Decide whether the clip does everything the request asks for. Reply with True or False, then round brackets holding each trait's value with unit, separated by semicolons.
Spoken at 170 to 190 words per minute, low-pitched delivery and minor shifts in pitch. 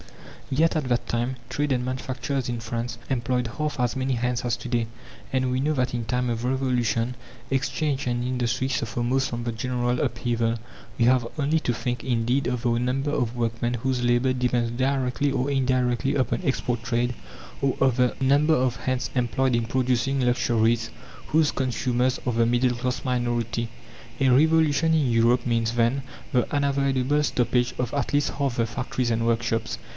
True (175 wpm; 125 Hz; 2.0 semitones)